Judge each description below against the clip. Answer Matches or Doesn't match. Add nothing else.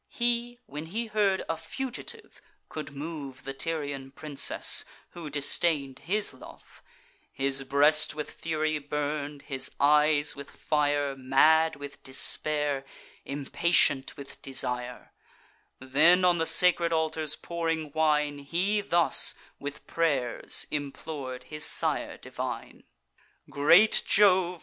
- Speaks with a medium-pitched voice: Matches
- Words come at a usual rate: Doesn't match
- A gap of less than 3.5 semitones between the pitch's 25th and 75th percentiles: Matches